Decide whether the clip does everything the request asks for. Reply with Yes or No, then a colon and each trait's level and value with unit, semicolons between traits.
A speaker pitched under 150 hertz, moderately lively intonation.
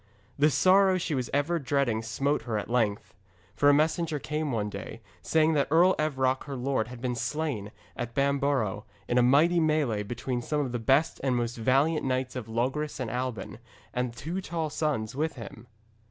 Yes: low, 135 Hz; average, 4.2 semitones